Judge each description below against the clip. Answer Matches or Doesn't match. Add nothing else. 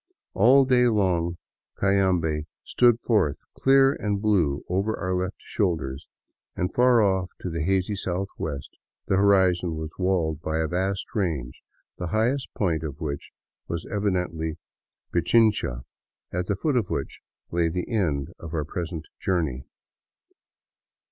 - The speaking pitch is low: Matches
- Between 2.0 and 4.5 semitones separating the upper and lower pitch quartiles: Matches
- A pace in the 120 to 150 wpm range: Matches